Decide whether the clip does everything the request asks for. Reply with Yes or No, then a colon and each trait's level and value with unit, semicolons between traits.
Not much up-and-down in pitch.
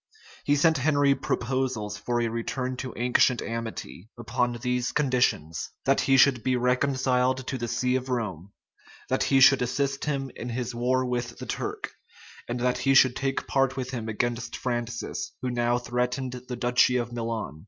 Yes: narrow, 1.8 semitones